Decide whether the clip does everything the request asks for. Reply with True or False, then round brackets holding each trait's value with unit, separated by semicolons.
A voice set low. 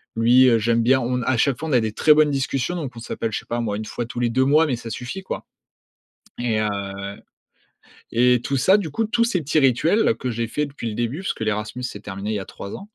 True (125 Hz)